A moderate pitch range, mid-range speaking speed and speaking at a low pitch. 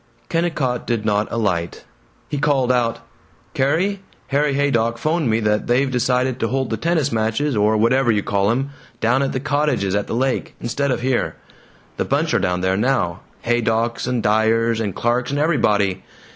Yes: average, 3.8 semitones; average, 175 wpm; low, 120 Hz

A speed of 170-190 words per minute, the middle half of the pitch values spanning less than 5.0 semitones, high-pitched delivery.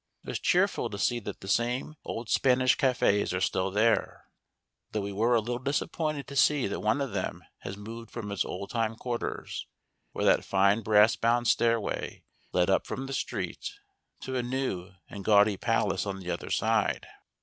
No: average, 185 wpm; average, 3.7 semitones; low, 115 Hz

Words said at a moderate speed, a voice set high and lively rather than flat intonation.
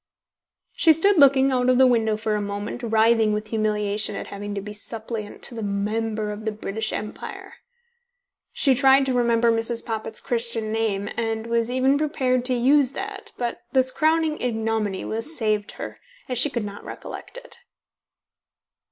No: average, 170 wpm; high, 230 Hz; average, 3.2 semitones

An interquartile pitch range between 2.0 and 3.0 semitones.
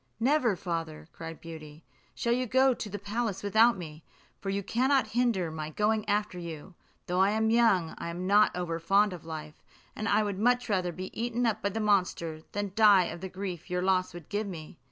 No: average, 4.4 semitones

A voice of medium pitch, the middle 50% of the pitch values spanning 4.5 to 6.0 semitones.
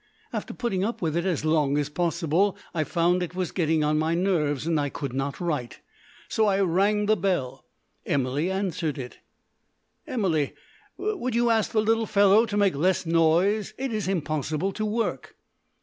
Yes: medium, 175 Hz; average, 4.9 semitones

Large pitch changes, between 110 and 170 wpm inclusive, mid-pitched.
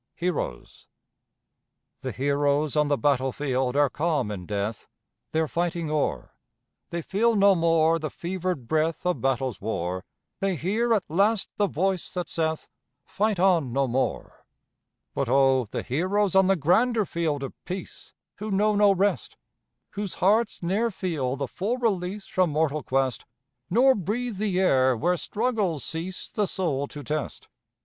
Yes: wide, 5.7 semitones; average, 150 wpm; medium, 170 Hz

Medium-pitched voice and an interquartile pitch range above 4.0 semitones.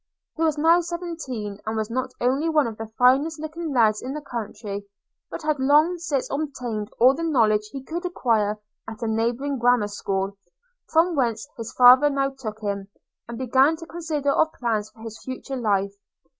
No: very high, 255 Hz; wide, 5.6 semitones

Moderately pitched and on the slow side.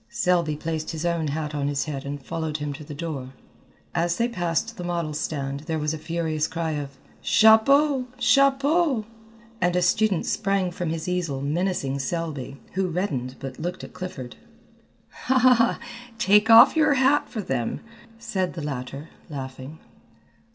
No: medium, 165 Hz; average, 155 wpm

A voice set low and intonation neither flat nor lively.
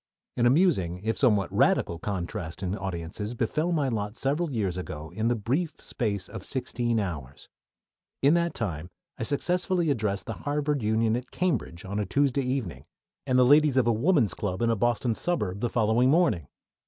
No: low, 115 Hz; wide, 5.9 semitones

